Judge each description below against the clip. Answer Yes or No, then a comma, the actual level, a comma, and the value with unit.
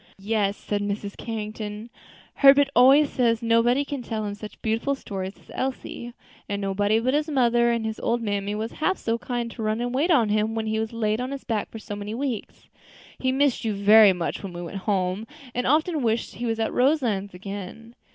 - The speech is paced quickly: Yes, fast, 210 wpm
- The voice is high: Yes, high, 225 Hz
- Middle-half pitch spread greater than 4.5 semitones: No, average, 3.2 semitones